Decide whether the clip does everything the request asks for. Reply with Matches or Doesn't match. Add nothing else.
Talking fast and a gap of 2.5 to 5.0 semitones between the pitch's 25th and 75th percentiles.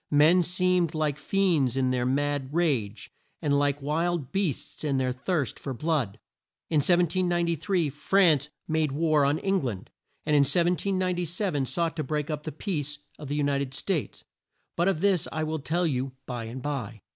Doesn't match